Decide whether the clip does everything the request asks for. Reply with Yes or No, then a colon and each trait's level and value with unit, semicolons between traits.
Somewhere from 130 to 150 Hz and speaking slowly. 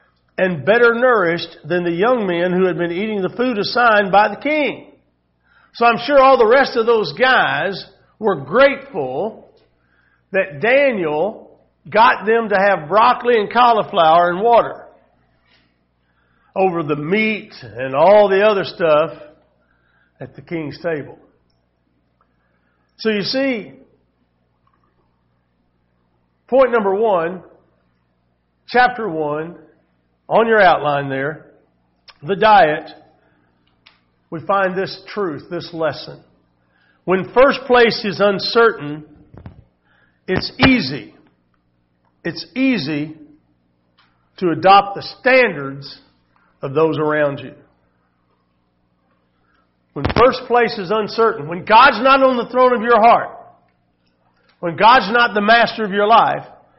No: medium, 160 Hz; slow, 115 wpm